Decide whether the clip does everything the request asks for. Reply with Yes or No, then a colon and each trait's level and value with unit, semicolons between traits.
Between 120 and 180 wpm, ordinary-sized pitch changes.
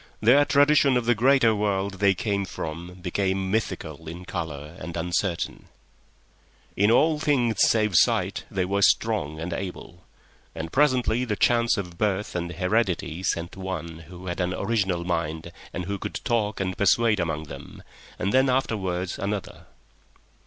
Yes: average, 140 wpm; average, 4.3 semitones